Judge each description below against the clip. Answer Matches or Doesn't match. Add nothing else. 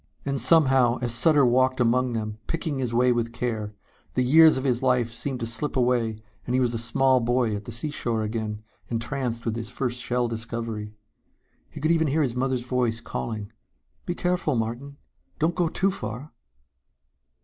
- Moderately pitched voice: Doesn't match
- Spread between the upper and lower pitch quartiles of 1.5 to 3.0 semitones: Matches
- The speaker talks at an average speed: Matches